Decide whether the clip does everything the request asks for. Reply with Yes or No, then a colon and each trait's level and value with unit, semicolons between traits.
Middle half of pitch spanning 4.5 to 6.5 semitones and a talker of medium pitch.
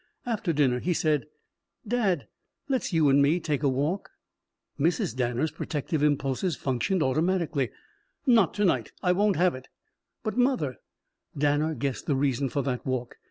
Yes: average, 5.1 semitones; medium, 150 Hz